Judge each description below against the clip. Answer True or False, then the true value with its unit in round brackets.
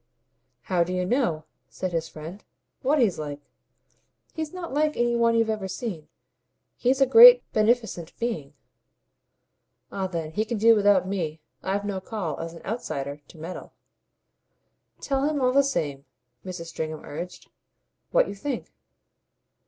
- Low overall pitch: False (200 Hz)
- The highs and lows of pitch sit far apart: True (6.6 semitones)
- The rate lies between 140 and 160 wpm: True (150 wpm)